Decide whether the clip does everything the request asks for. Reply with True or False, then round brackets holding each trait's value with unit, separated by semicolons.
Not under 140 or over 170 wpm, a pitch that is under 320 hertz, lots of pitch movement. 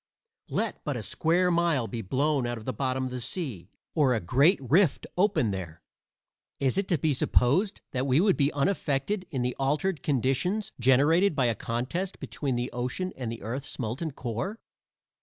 False (180 wpm; 135 Hz; 5.7 semitones)